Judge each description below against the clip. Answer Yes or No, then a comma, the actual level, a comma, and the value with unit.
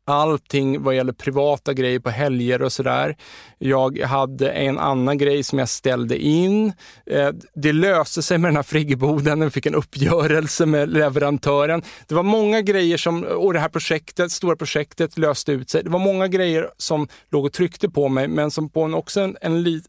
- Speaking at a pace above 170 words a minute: Yes, average, 190 wpm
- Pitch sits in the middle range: Yes, medium, 150 Hz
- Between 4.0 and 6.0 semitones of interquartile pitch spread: No, average, 3.2 semitones